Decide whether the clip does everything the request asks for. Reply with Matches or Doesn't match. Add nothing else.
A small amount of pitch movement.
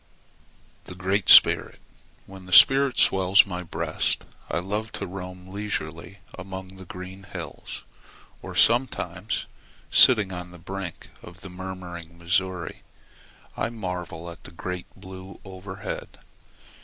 Matches